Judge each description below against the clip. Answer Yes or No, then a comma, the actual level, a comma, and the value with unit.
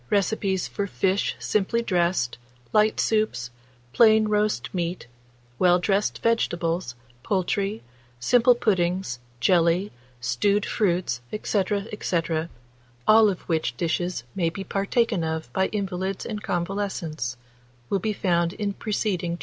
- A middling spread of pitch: Yes, average, 3.5 semitones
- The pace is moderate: No, slow, 130 wpm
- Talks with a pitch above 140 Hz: Yes, high, 190 Hz